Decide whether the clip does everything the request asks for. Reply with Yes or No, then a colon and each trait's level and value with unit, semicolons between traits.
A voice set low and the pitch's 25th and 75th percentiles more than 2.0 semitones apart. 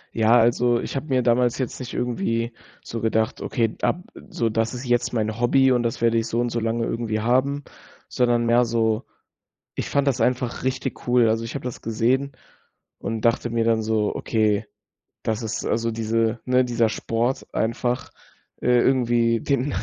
No: low, 115 Hz; narrow, 1.6 semitones